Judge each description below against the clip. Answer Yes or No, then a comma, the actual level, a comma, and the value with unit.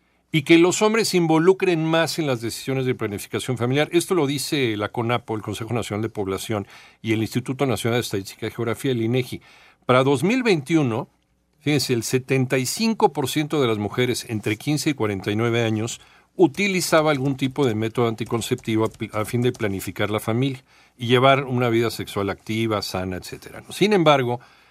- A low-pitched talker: Yes, low, 120 Hz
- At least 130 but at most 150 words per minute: No, average, 170 wpm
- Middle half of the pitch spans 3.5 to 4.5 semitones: No, average, 5.1 semitones